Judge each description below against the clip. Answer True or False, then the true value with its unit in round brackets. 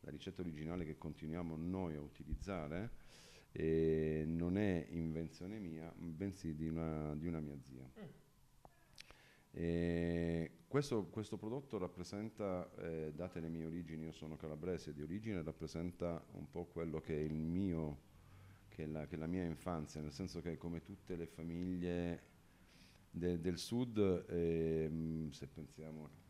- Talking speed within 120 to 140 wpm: False (150 wpm)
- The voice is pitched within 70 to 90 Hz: True (85 Hz)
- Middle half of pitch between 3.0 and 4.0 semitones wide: False (2.4 semitones)